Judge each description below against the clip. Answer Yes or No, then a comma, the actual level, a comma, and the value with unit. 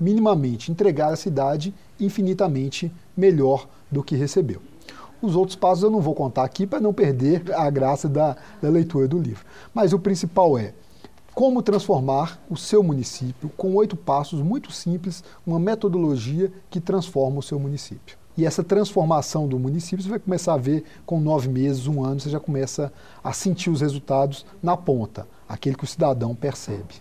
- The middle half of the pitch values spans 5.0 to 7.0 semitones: Yes, wide, 5.5 semitones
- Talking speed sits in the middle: Yes, average, 170 wpm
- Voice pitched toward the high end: No, medium, 155 Hz